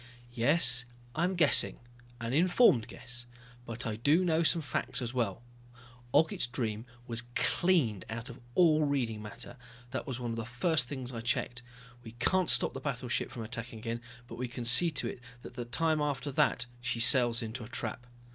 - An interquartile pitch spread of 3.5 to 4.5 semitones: Yes, average, 3.9 semitones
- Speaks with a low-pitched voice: Yes, low, 125 Hz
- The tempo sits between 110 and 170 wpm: No, average, 185 wpm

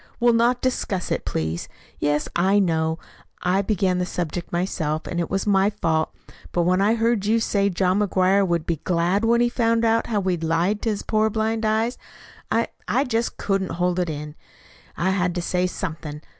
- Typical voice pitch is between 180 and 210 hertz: Yes, high, 190 Hz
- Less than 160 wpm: No, average, 195 wpm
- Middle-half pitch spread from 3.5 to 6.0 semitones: Yes, average, 4.1 semitones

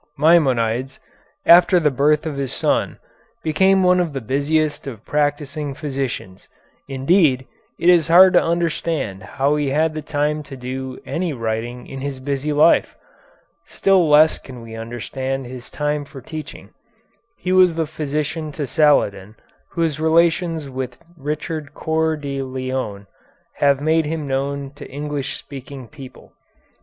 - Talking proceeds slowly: No, average, 145 wpm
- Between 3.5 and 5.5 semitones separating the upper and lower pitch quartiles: No, average, 3.1 semitones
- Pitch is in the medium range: Yes, medium, 145 Hz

